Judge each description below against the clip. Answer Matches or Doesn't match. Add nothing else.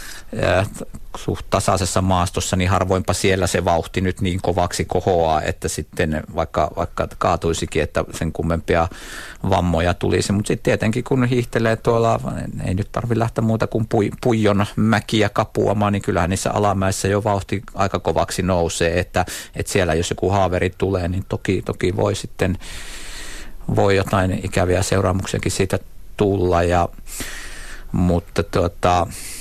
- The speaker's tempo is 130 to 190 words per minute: Matches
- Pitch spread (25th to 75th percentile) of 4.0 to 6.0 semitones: Doesn't match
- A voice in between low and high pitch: Doesn't match